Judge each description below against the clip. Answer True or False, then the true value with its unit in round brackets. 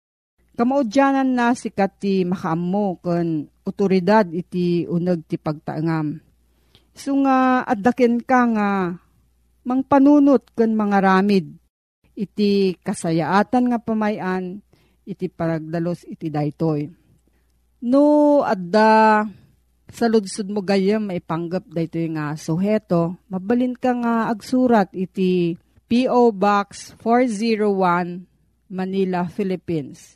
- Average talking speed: False (100 wpm)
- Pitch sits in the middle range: False (195 Hz)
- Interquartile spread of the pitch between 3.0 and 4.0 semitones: False (5.1 semitones)